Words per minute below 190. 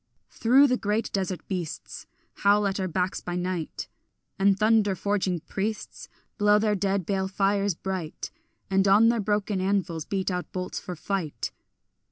Yes: average, 155 wpm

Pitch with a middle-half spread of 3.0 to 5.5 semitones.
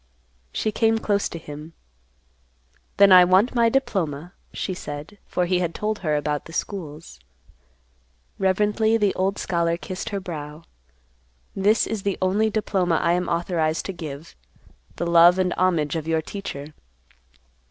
Yes: average, 3.9 semitones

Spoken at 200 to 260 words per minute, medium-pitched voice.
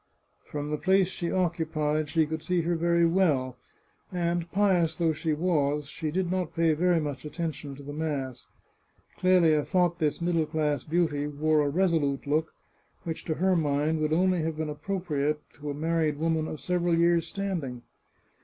No: average, 180 wpm; medium, 160 Hz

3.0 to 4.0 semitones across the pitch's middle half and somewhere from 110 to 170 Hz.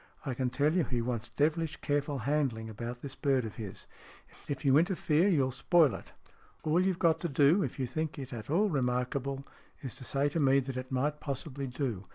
Yes: average, 3.4 semitones; medium, 140 Hz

